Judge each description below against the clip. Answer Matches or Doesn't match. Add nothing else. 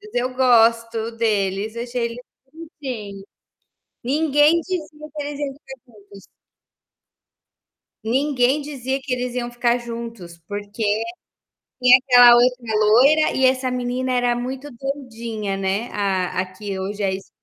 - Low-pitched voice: Doesn't match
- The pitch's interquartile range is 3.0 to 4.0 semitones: Matches